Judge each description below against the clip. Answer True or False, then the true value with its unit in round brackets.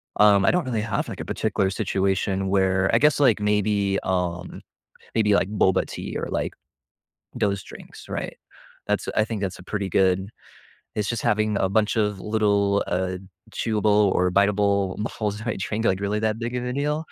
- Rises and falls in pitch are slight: True (1.9 semitones)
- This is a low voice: True (100 Hz)